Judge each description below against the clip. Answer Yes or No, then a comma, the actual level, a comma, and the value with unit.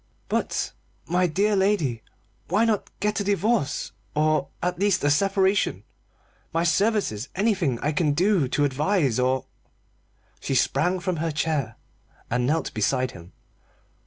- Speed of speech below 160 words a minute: Yes, average, 140 wpm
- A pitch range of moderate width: No, wide, 6.3 semitones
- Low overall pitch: No, medium, 165 Hz